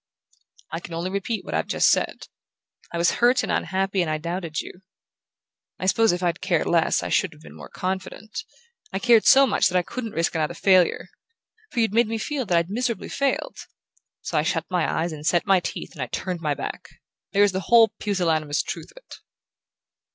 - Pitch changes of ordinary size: Yes, average, 4.7 semitones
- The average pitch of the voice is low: No, medium, 185 Hz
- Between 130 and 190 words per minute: No, fast, 205 wpm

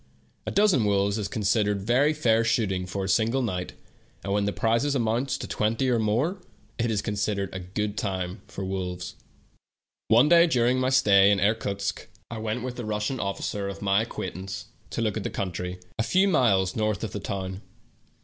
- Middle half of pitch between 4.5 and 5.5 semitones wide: No, average, 3.3 semitones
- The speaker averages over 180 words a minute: Yes, average, 190 wpm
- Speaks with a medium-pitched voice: No, low, 105 Hz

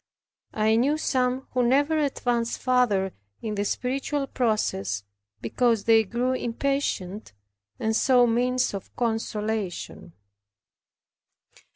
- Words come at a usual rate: No, slow, 100 wpm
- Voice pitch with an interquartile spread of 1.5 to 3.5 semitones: Yes, average, 3.1 semitones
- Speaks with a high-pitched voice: Yes, high, 235 Hz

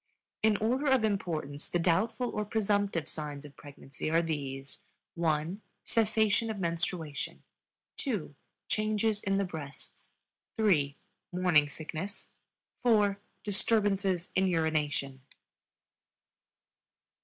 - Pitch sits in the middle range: Yes, medium, 180 Hz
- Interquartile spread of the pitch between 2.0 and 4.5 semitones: No, wide, 5.5 semitones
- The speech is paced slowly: Yes, slow, 100 wpm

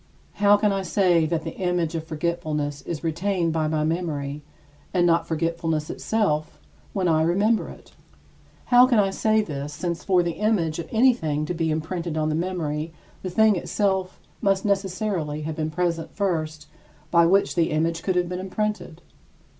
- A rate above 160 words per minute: Yes, average, 170 wpm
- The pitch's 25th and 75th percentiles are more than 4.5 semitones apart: No, average, 3.5 semitones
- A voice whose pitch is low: No, medium, 170 Hz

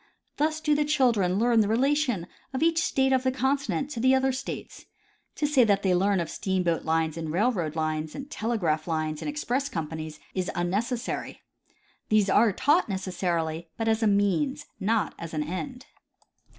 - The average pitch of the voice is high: Yes, high, 215 Hz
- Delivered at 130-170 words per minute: No, average, 180 wpm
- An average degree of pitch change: No, wide, 7.6 semitones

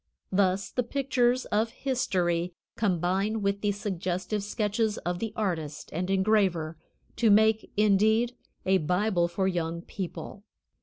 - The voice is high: Yes, high, 200 Hz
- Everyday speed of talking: No, slow, 130 wpm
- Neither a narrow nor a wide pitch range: Yes, average, 3.4 semitones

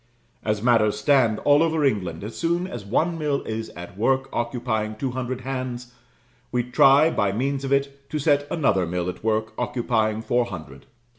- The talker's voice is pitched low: Yes, low, 125 Hz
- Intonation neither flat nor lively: Yes, average, 4.3 semitones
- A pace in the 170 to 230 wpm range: Yes, average, 175 wpm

